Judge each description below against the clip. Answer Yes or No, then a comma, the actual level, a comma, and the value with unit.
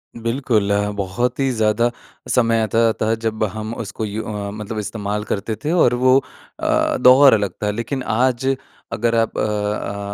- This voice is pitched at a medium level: No, low, 110 Hz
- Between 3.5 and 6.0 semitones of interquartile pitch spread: No, narrow, 2.6 semitones